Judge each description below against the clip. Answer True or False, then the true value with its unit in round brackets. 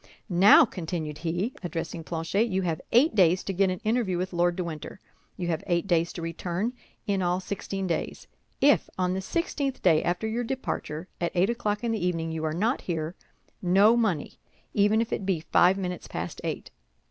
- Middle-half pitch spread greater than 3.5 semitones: True (3.9 semitones)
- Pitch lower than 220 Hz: True (185 Hz)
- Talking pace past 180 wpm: True (190 wpm)